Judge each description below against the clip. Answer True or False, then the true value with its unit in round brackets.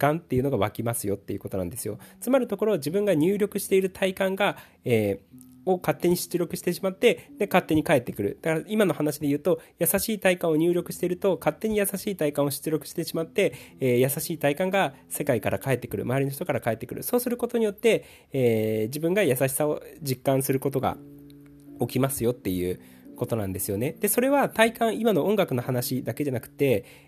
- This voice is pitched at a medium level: True (150 Hz)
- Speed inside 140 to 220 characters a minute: False (430 characters per minute)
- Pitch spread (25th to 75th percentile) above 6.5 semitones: True (7.1 semitones)